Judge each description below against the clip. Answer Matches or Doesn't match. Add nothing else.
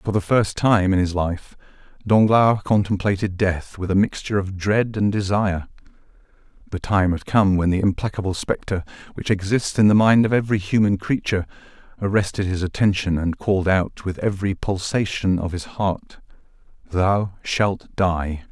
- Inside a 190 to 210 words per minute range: Doesn't match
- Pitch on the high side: Doesn't match